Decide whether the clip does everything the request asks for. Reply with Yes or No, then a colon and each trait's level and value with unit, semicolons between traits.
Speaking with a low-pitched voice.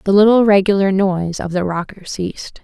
No: high, 195 Hz